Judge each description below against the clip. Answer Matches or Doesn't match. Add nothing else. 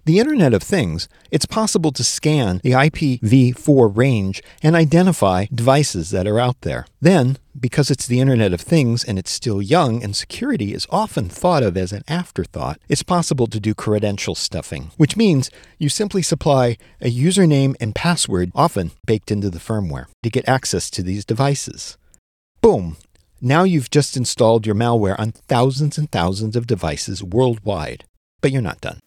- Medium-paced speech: Matches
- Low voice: Matches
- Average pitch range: Doesn't match